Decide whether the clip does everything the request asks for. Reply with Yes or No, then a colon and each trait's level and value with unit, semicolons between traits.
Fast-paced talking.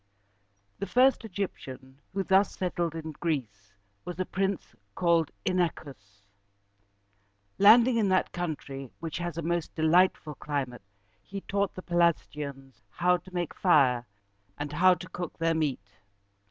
No: average, 140 wpm